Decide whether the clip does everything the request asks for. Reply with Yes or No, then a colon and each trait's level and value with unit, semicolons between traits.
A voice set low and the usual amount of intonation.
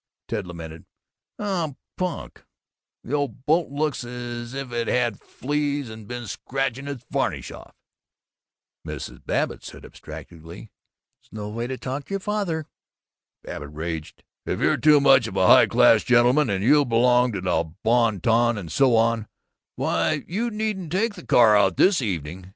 No: low, 120 Hz; wide, 5.7 semitones